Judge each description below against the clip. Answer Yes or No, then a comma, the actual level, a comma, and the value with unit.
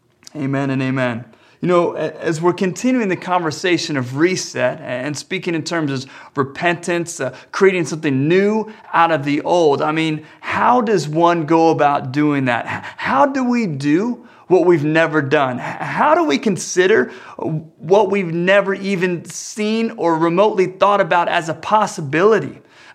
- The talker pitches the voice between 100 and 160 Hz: No, medium, 170 Hz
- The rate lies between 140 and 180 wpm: Yes, average, 155 wpm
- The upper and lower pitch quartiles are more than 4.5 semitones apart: No, average, 4.2 semitones